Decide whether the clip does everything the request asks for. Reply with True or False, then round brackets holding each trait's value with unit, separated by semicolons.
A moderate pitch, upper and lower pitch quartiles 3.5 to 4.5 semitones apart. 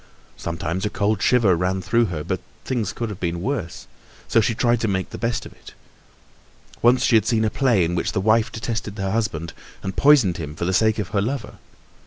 False (105 Hz; 3.9 semitones)